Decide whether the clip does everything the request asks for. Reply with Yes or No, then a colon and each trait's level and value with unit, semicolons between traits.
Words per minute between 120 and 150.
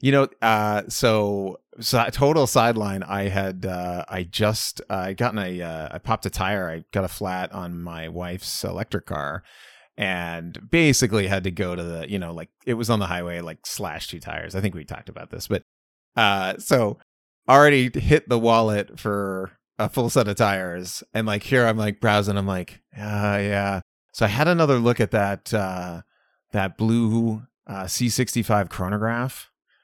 No: average, 185 wpm